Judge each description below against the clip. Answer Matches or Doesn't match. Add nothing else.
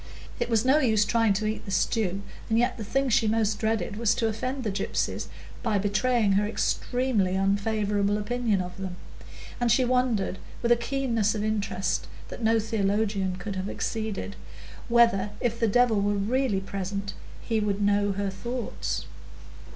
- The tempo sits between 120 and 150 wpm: Doesn't match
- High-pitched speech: Matches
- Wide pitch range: Doesn't match